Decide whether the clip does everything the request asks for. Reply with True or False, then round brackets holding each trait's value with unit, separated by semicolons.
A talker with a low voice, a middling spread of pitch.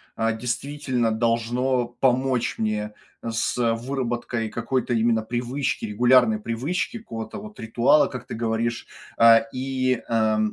False (120 Hz; 2.2 semitones)